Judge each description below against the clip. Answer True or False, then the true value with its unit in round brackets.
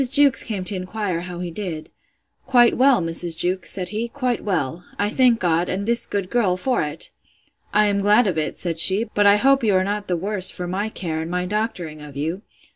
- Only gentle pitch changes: False (3.6 semitones)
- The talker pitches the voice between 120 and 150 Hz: False (190 Hz)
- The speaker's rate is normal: False (215 wpm)